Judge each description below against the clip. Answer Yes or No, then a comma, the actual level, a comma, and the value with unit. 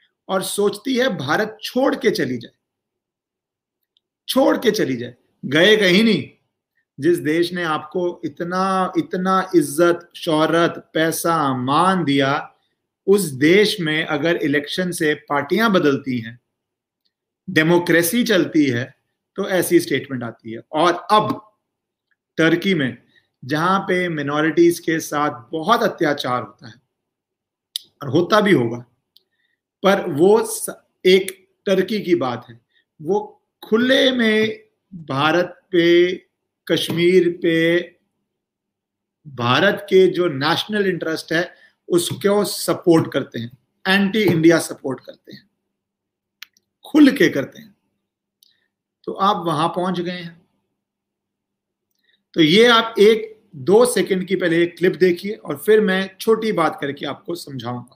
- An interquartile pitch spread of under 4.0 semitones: No, average, 4.9 semitones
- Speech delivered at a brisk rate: No, average, 120 wpm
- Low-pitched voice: No, medium, 175 Hz